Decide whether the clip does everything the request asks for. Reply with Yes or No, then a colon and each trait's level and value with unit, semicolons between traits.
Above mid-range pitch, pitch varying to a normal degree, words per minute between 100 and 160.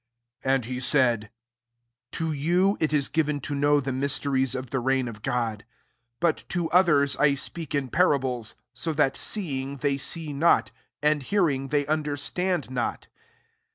No: medium, 140 Hz; average, 3.0 semitones; average, 145 wpm